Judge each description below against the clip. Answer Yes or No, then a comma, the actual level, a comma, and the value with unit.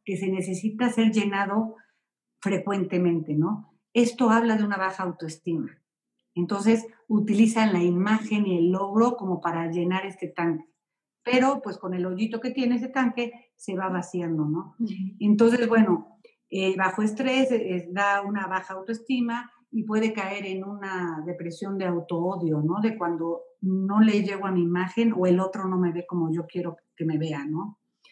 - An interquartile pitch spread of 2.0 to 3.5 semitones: No, average, 4.0 semitones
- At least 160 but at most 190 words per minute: Yes, average, 170 wpm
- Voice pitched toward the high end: Yes, high, 195 Hz